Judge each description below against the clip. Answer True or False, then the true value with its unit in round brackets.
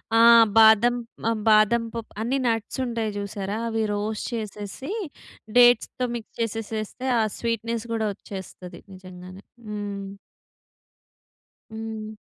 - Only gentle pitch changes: True (2.1 semitones)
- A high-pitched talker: True (220 Hz)